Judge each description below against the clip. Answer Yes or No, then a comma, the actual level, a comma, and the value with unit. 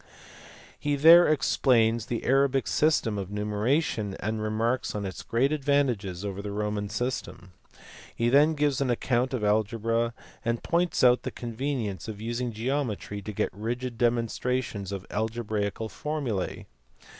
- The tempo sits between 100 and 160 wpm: Yes, average, 140 wpm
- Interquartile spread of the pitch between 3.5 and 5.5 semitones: Yes, average, 3.9 semitones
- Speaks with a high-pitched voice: No, low, 115 Hz